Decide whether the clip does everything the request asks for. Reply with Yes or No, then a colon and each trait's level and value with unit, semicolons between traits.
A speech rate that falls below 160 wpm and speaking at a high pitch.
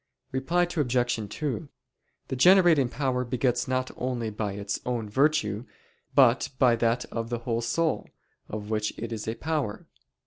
No: average, 150 wpm; low, 125 Hz